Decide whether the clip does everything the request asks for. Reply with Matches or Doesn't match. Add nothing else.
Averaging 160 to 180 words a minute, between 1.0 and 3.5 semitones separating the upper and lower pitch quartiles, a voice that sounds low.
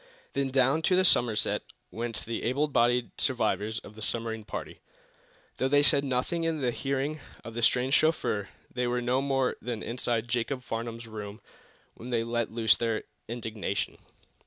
Matches